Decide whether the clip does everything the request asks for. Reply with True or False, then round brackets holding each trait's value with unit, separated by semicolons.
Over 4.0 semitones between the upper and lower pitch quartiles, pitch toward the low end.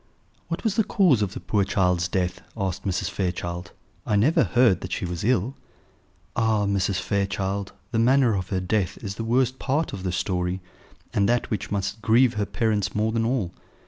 False (3.7 semitones; 100 Hz)